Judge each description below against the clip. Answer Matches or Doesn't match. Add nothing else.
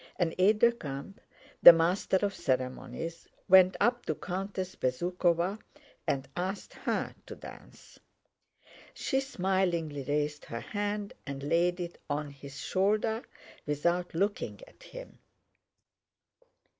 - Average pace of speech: Doesn't match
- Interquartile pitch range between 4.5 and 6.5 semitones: Matches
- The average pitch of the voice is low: Doesn't match